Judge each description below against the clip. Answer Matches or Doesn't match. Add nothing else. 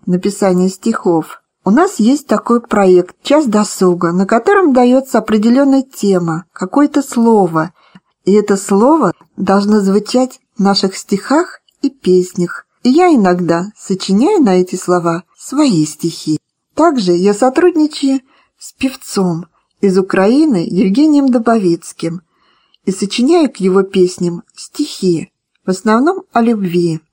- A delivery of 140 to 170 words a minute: Doesn't match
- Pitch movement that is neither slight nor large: Doesn't match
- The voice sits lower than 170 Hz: Doesn't match